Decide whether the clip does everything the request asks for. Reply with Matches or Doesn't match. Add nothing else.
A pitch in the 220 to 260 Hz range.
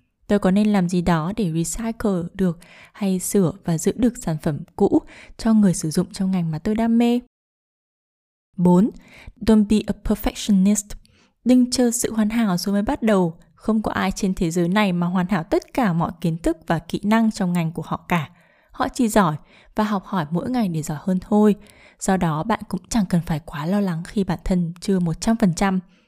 Doesn't match